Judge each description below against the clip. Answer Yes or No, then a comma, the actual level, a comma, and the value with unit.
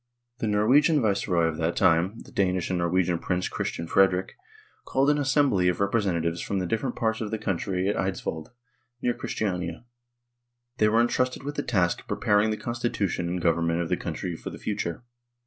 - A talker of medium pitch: No, very low, 95 Hz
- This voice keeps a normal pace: Yes, average, 180 wpm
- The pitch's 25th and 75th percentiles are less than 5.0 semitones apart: Yes, average, 4.5 semitones